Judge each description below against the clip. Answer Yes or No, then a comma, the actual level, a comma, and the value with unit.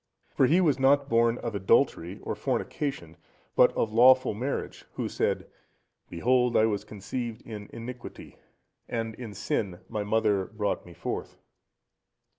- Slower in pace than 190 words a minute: Yes, average, 140 wpm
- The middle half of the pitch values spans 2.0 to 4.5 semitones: Yes, average, 3.6 semitones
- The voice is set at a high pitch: No, low, 115 Hz